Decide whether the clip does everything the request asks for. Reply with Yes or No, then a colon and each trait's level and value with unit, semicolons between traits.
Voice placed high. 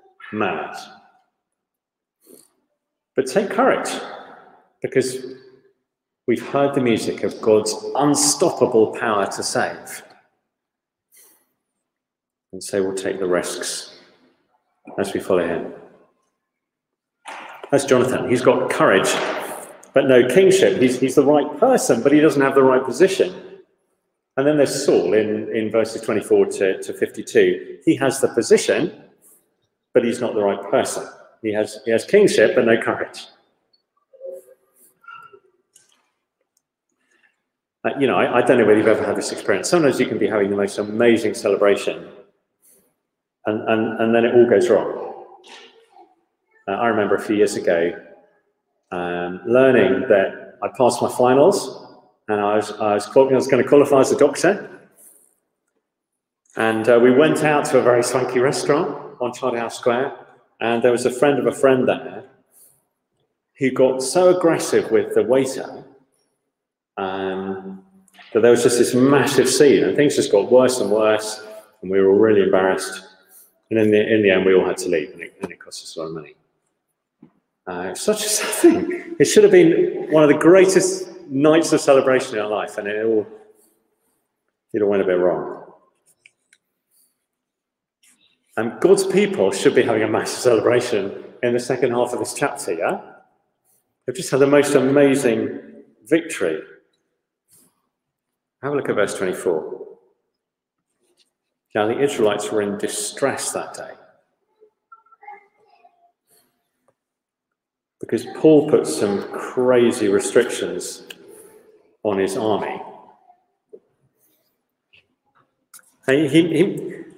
No: medium, 145 Hz